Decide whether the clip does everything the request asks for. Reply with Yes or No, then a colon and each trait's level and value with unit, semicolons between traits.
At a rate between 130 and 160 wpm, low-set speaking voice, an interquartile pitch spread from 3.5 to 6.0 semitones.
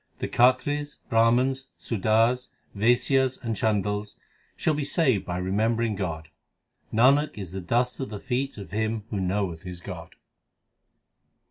Yes: slow, 135 wpm; low, 115 Hz; average, 4.4 semitones